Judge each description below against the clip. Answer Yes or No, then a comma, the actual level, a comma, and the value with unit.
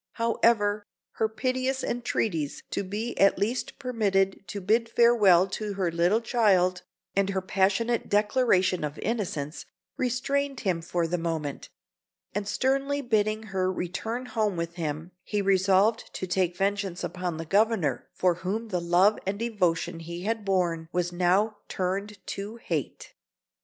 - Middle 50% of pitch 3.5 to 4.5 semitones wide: Yes, average, 4.0 semitones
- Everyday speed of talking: Yes, average, 145 wpm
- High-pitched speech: Yes, high, 195 Hz